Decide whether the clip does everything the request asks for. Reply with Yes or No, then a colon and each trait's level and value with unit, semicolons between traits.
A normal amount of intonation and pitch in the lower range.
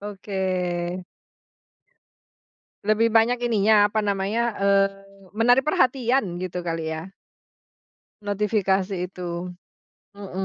No: average, 3.3 semitones; high, 205 Hz